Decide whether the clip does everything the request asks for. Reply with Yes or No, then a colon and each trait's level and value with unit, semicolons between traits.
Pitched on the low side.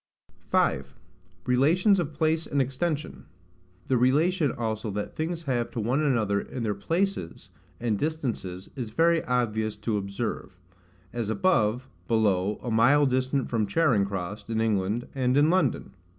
Yes: low, 120 Hz